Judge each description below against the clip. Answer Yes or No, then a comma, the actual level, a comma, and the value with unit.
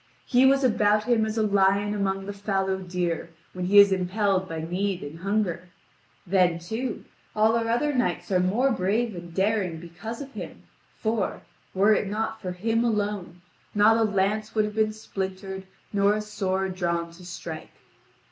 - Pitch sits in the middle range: No, high, 200 Hz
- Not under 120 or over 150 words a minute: No, average, 175 wpm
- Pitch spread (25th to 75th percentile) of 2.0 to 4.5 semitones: Yes, average, 3.0 semitones